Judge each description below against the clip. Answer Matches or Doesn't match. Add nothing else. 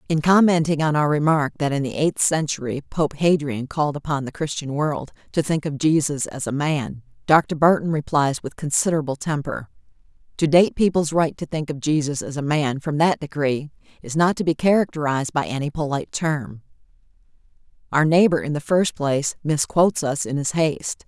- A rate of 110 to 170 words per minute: Doesn't match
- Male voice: Doesn't match